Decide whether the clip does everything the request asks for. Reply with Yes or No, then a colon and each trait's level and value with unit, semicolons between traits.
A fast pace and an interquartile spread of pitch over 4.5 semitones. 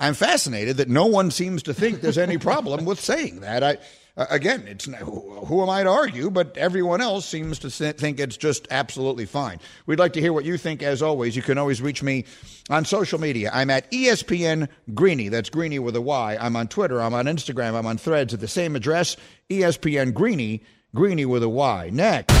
Yes: fast, 210 wpm; average, 5.0 semitones